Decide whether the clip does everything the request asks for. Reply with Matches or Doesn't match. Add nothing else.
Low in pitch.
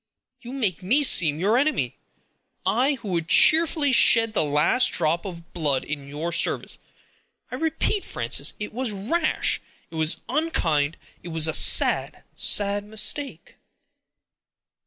Doesn't match